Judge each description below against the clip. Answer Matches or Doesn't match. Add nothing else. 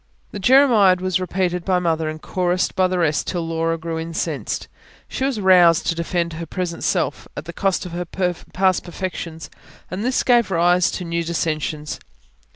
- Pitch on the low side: Doesn't match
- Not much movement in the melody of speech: Matches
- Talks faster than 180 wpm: Doesn't match